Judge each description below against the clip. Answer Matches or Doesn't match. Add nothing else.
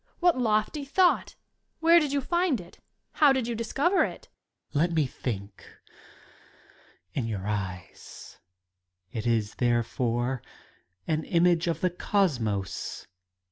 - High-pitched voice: Doesn't match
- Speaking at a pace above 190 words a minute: Doesn't match